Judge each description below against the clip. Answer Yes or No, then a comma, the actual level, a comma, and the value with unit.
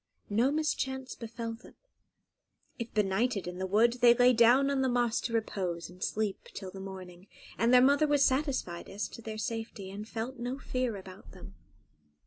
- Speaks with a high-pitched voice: Yes, high, 230 Hz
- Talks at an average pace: Yes, average, 180 wpm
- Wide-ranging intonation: No, average, 4.4 semitones